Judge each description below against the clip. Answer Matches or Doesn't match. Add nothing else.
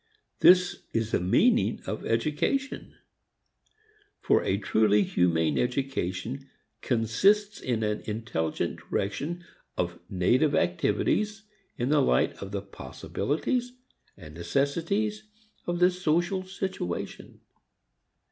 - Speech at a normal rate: Doesn't match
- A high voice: Doesn't match